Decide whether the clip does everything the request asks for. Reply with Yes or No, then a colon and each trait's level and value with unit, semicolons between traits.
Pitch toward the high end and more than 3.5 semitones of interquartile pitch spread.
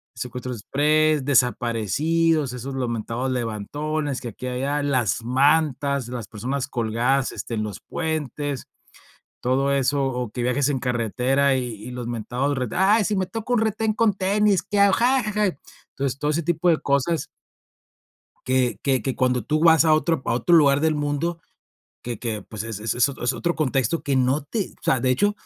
No: low, 135 Hz; average, 4.0 semitones